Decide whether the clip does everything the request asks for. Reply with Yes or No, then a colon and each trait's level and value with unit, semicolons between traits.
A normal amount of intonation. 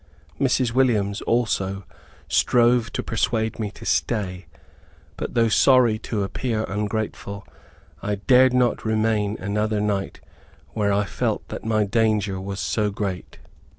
No: narrow, 2.3 semitones